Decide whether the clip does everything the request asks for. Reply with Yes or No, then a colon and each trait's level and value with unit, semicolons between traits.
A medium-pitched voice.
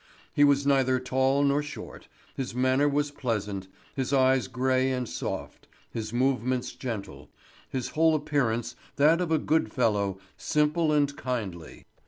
No: low, 130 Hz